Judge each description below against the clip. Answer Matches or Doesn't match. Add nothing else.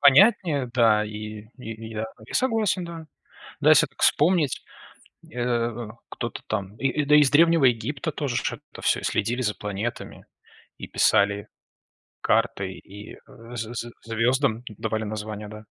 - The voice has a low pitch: Matches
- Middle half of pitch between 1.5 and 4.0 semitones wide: Doesn't match